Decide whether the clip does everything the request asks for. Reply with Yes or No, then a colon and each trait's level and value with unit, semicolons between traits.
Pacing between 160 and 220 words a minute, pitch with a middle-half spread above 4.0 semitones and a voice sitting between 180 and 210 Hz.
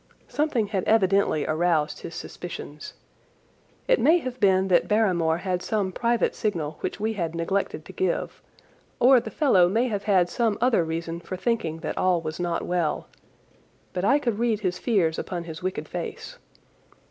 Yes: average, 170 wpm; average, 4.8 semitones; high, 190 Hz